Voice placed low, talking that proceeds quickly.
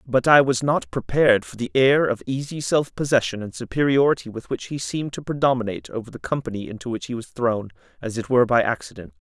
Yes: low, 125 Hz; fast, 215 wpm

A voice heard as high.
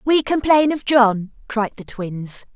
Yes: high, 240 Hz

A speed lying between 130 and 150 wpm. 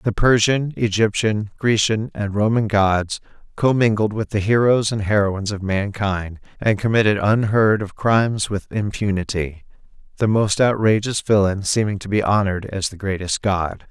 Yes: average, 145 wpm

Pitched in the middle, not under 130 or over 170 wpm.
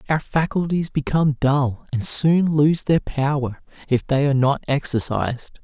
Yes: medium, 145 Hz; average, 150 wpm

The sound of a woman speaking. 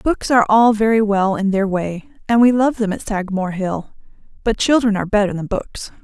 Yes: female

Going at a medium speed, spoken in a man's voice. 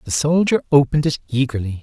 Yes: average, 165 wpm; male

